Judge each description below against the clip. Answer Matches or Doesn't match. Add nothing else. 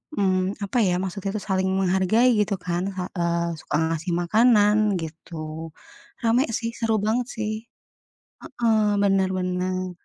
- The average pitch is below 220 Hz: Matches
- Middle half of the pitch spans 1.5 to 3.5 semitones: Matches